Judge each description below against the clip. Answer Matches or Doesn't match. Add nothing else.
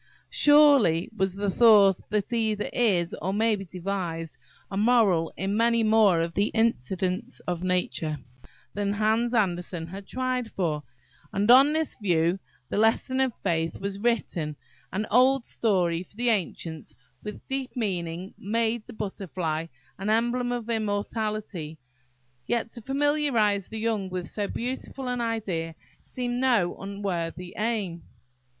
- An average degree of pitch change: Matches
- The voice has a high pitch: Matches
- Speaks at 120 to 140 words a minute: Matches